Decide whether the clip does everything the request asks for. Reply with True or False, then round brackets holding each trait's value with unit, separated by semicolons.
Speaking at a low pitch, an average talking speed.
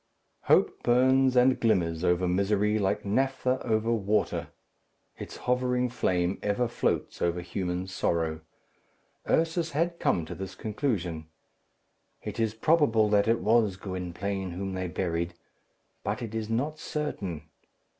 False (105 Hz; 130 wpm)